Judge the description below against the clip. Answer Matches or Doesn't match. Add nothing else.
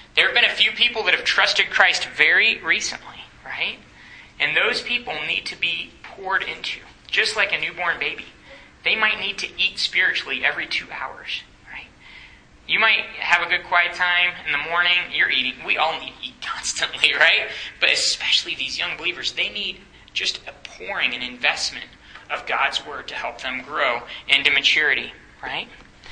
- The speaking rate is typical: Matches